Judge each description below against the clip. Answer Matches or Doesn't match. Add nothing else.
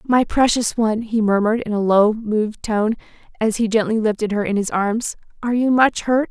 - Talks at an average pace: Doesn't match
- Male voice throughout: Doesn't match